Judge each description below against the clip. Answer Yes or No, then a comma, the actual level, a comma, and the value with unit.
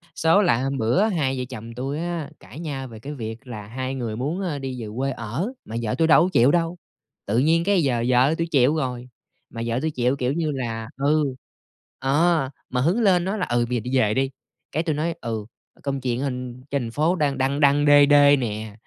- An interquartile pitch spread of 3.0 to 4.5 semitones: Yes, average, 4.2 semitones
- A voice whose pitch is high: No, low, 135 Hz